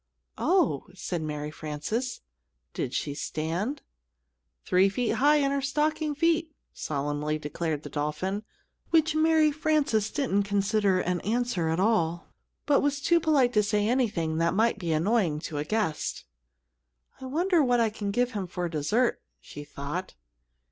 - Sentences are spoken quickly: No, average, 150 wpm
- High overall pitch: Yes, high, 210 Hz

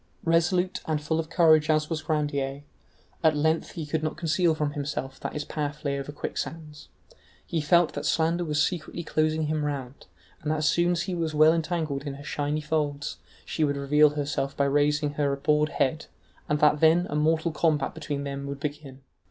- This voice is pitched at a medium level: Yes, medium, 150 Hz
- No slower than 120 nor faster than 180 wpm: No, average, 195 wpm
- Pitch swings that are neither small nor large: No, narrow, 1.6 semitones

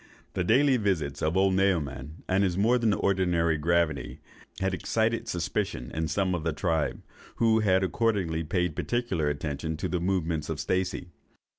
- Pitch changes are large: No, average, 3.6 semitones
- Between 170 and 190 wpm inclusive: No, average, 160 wpm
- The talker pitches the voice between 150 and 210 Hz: No, very low, 90 Hz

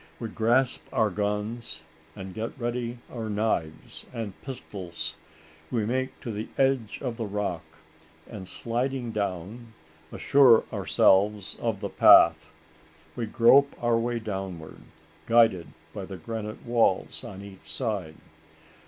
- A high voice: No, low, 110 Hz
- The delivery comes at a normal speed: No, slow, 125 wpm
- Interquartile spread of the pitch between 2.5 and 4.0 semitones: Yes, average, 3.6 semitones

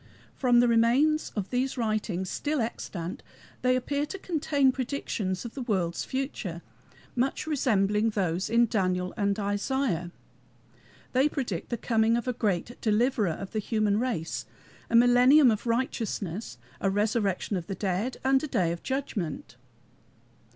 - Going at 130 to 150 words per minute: Yes, average, 145 wpm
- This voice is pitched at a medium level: No, high, 225 Hz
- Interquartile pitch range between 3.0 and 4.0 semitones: No, average, 4.8 semitones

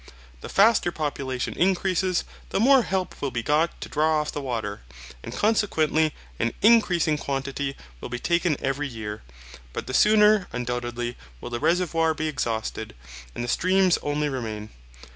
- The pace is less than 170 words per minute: Yes, average, 155 wpm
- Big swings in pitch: Yes, wide, 6.7 semitones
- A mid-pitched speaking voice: Yes, medium, 150 Hz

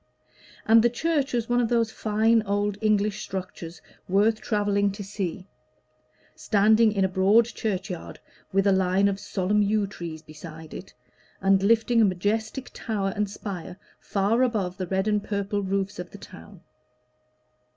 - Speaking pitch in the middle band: No, high, 200 Hz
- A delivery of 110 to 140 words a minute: No, average, 155 wpm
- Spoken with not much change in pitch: Yes, narrow, 2.3 semitones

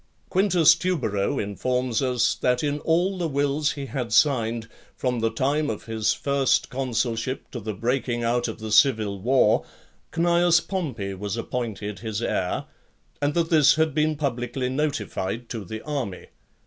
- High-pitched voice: No, low, 125 Hz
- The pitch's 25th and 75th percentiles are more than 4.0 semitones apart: Yes, average, 4.9 semitones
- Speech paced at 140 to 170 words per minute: Yes, average, 155 wpm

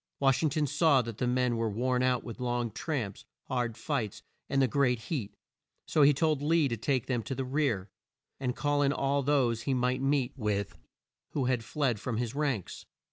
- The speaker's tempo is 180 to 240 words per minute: Yes, average, 200 wpm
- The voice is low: Yes, low, 130 Hz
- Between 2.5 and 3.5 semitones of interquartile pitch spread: Yes, average, 3.2 semitones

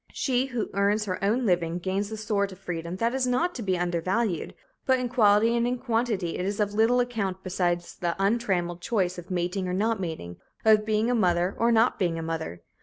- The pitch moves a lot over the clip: No, average, 4.5 semitones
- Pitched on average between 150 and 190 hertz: No, high, 200 Hz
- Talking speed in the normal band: No, fast, 215 wpm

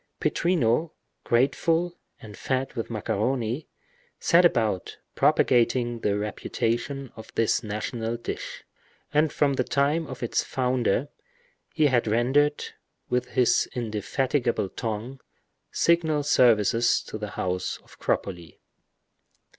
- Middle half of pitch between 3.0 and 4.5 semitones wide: Yes, average, 4.2 semitones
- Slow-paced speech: Yes, slow, 110 wpm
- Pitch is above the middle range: No, low, 120 Hz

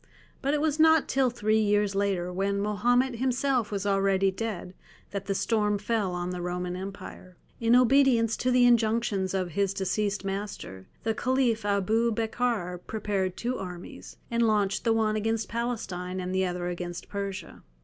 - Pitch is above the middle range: Yes, high, 205 Hz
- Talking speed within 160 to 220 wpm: Yes, average, 165 wpm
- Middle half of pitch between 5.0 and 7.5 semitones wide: No, average, 3.6 semitones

